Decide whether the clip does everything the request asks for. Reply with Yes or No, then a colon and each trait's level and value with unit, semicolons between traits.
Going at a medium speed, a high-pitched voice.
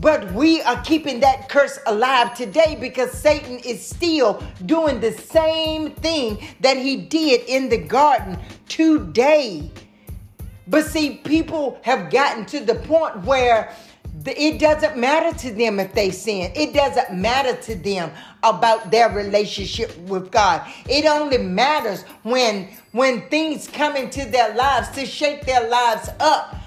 Yes: average, 145 wpm; very high, 260 Hz